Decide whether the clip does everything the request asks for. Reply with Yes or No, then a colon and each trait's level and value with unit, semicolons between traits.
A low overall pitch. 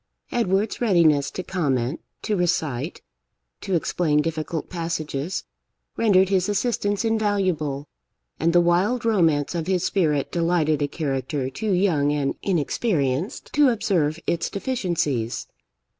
No: medium, 170 Hz